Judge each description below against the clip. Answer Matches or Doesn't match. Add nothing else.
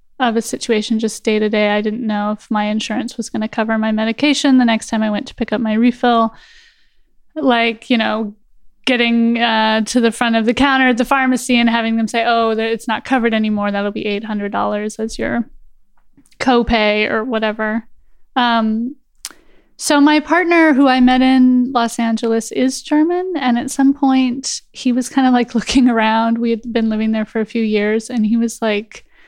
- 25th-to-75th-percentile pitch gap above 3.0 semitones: Doesn't match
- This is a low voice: Doesn't match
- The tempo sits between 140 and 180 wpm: Doesn't match